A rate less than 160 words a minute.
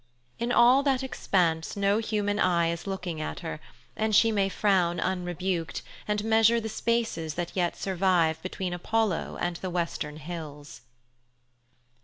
Yes: average, 145 wpm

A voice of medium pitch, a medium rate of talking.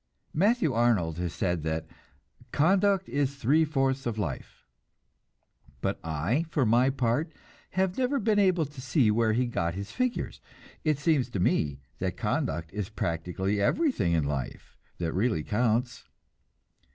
No: low, 120 Hz; average, 145 wpm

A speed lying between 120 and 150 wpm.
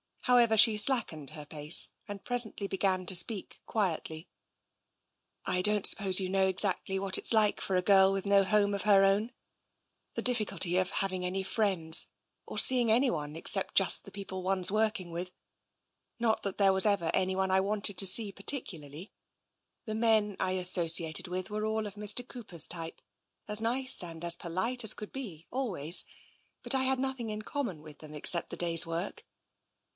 No: average, 185 wpm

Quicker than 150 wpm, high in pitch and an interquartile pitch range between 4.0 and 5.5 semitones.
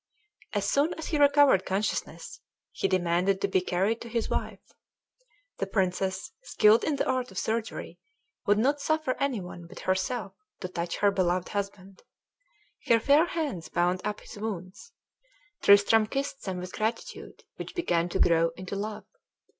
Yes: average, 160 wpm; high, 205 Hz; average, 5.2 semitones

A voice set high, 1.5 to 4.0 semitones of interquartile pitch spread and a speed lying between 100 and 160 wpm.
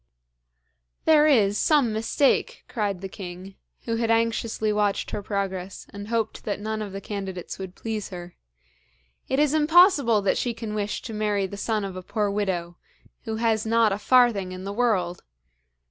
No: high, 210 Hz; average, 2.7 semitones; average, 175 wpm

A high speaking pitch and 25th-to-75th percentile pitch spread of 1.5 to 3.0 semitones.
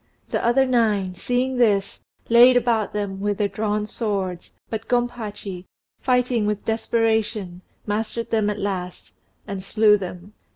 Yes: high, 210 Hz; average, 2.7 semitones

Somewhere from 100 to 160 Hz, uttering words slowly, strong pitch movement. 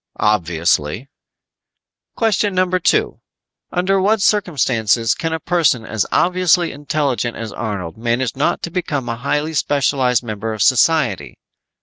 Yes: low, 135 Hz; slow, 125 wpm; wide, 7.7 semitones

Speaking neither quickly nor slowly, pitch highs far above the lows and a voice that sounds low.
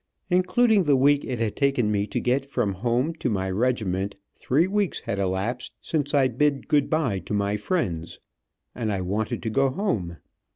Yes: average, 180 wpm; wide, 6.3 semitones; low, 125 Hz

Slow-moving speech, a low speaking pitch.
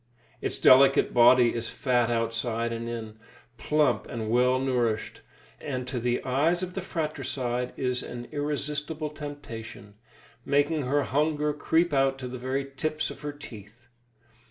No: average, 145 wpm; low, 130 Hz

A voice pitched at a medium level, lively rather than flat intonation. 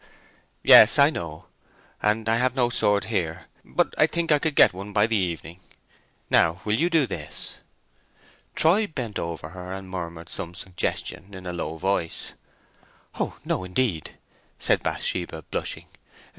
No: very low, 95 Hz; wide, 5.7 semitones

